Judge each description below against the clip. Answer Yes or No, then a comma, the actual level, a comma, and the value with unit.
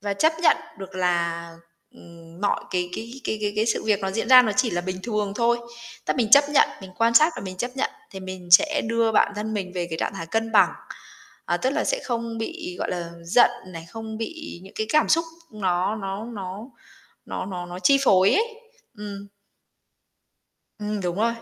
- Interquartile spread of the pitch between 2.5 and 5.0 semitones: Yes, average, 4.1 semitones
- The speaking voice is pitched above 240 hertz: No, high, 210 Hz